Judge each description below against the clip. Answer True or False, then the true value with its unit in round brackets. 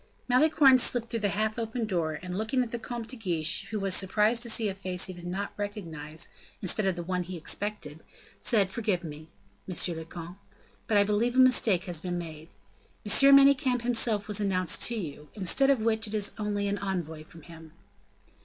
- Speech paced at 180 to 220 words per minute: True (200 wpm)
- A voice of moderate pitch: False (200 Hz)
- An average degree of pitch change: True (4.5 semitones)